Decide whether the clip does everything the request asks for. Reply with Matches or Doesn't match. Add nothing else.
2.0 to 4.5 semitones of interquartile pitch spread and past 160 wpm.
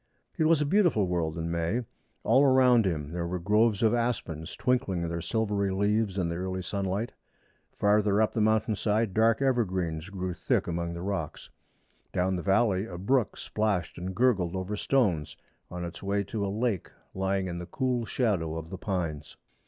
Matches